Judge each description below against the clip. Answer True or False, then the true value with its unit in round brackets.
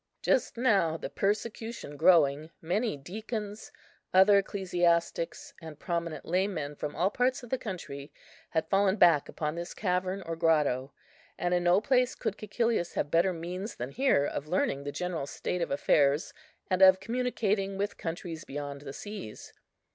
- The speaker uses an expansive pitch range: False (4.7 semitones)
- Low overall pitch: False (180 Hz)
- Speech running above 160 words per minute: False (155 wpm)